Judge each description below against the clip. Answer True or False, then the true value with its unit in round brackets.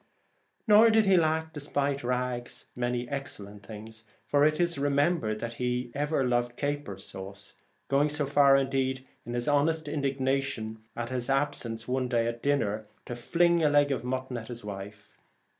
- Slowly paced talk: False (175 wpm)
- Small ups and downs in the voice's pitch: False (3.5 semitones)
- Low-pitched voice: True (130 Hz)